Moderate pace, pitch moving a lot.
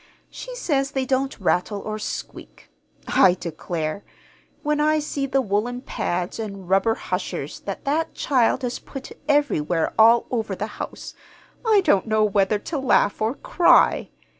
Yes: average, 150 wpm; wide, 5.7 semitones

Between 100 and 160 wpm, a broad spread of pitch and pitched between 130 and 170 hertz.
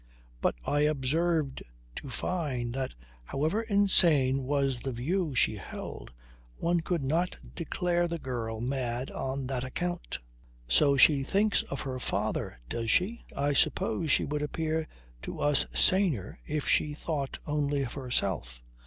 No: average, 145 wpm; average, 4.4 semitones; medium, 140 Hz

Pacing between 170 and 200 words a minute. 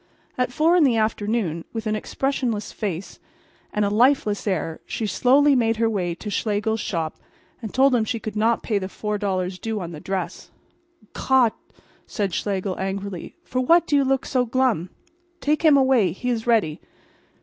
Yes: average, 175 wpm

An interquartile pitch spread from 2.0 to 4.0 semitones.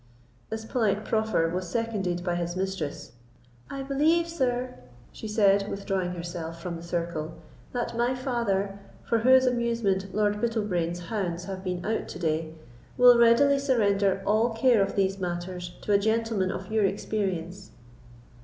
No: average, 4.5 semitones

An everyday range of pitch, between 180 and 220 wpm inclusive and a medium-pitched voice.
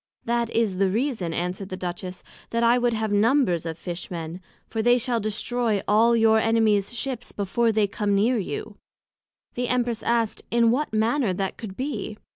No: average, 3.3 semitones; average, 185 wpm; high, 220 Hz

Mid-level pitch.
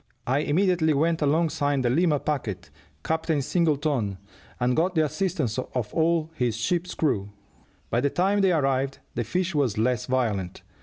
Yes: medium, 145 Hz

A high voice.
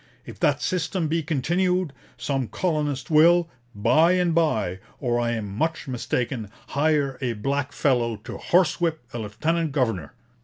No: medium, 145 Hz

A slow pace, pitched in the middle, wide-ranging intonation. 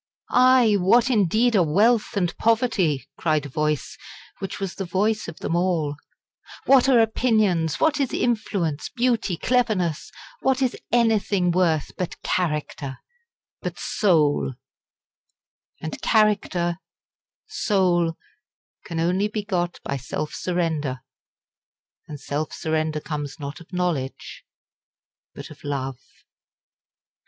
Yes: slow, 115 wpm; medium, 180 Hz; wide, 5.9 semitones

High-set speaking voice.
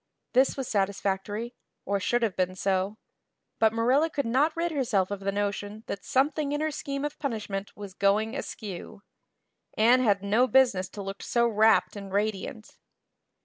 Yes: high, 215 Hz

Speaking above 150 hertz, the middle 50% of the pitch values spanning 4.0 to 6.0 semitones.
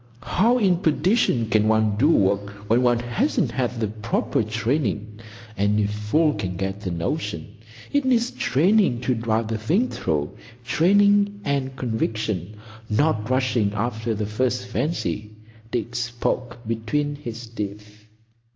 No: low, 115 Hz; average, 5.3 semitones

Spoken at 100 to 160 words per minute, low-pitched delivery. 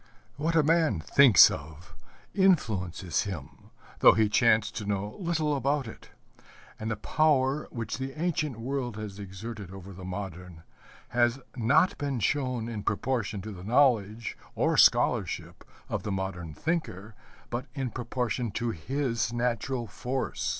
Yes: average, 145 wpm; low, 115 Hz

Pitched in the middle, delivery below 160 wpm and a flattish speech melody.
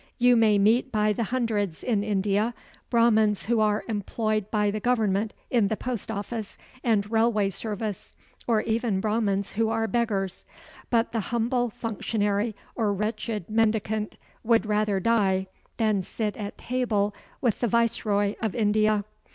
No: high, 215 Hz; average, 145 wpm; narrow, 2.0 semitones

